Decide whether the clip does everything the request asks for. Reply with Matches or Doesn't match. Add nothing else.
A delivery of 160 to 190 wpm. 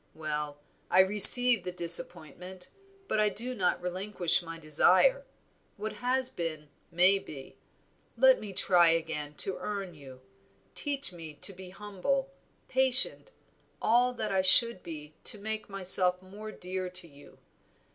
Doesn't match